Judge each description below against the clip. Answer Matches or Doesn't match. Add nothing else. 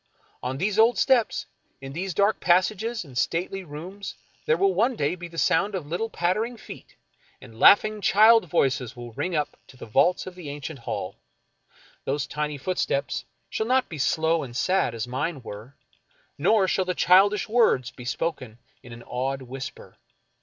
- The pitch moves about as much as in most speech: Doesn't match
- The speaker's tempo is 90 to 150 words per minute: Doesn't match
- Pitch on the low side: Doesn't match